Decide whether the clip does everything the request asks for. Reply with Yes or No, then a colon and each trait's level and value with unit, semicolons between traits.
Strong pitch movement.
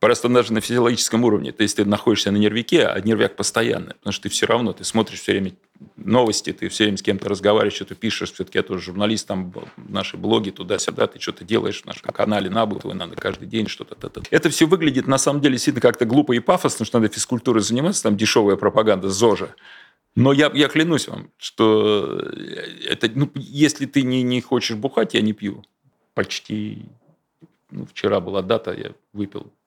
No: average, 4.4 semitones